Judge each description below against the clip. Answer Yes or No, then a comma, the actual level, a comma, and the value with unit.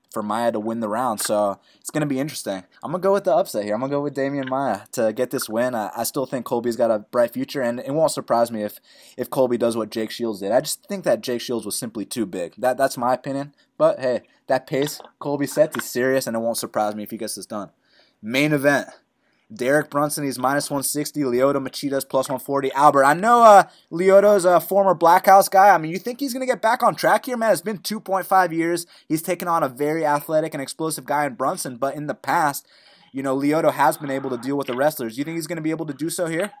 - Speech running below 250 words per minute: No, fast, 260 wpm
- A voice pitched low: No, medium, 145 Hz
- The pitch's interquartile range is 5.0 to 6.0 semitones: Yes, average, 5.3 semitones